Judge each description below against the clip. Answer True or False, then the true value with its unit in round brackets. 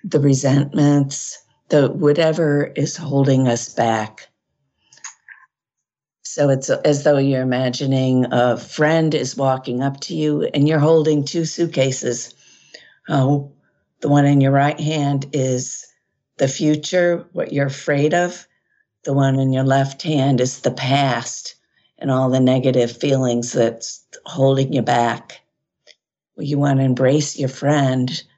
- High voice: False (140 Hz)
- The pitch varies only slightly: True (2.3 semitones)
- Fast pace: False (135 wpm)